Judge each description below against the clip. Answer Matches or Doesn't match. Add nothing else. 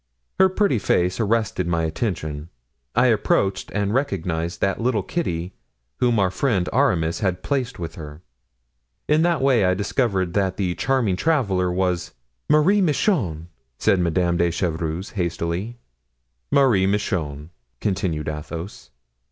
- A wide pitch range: Matches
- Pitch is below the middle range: Matches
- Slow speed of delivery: Matches